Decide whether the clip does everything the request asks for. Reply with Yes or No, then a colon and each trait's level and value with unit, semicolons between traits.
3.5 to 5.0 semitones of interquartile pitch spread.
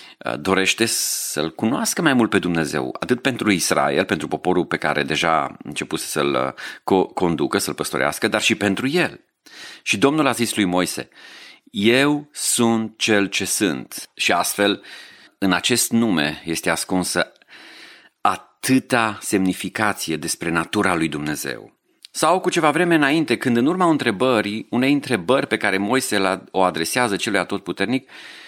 No: wide, 5.4 semitones